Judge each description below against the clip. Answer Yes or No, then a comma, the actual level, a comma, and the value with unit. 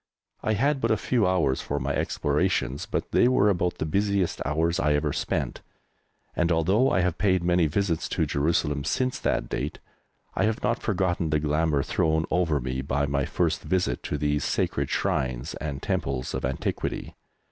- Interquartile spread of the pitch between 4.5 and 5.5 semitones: Yes, average, 4.9 semitones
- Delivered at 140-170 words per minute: No, average, 180 wpm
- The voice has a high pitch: No, very low, 80 Hz